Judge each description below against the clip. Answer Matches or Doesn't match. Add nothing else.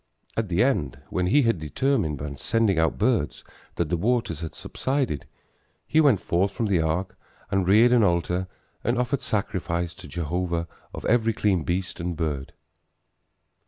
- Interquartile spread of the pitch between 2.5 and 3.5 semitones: Doesn't match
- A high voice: Doesn't match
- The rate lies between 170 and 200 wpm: Doesn't match